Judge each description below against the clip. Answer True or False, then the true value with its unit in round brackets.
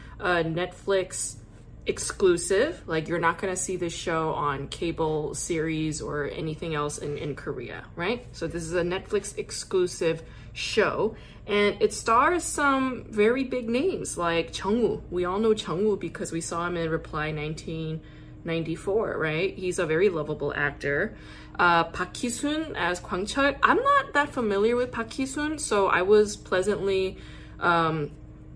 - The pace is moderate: True (155 wpm)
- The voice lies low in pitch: False (180 Hz)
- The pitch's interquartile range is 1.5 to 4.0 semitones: False (5.3 semitones)